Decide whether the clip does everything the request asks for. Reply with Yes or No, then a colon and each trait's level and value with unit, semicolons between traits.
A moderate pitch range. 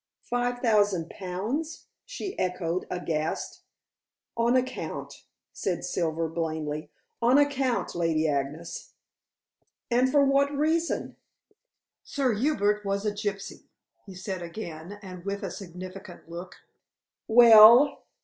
No: wide, 6.1 semitones